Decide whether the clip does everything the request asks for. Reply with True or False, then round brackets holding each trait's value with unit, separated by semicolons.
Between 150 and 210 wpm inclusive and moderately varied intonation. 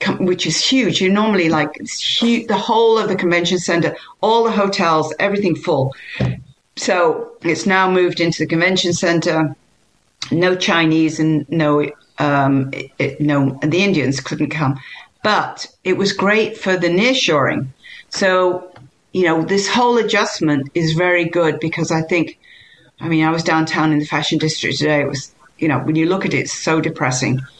True (180 wpm; 3.5 semitones)